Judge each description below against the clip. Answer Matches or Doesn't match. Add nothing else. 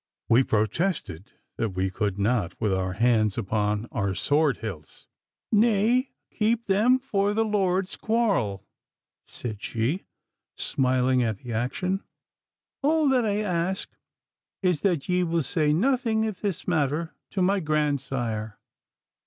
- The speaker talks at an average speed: Doesn't match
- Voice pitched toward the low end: Doesn't match